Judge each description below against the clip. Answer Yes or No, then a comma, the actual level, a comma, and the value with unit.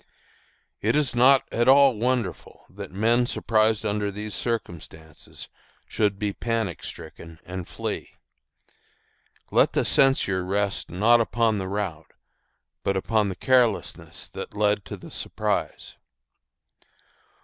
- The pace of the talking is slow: Yes, slow, 120 wpm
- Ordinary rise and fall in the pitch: Yes, average, 3.4 semitones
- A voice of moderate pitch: No, low, 105 Hz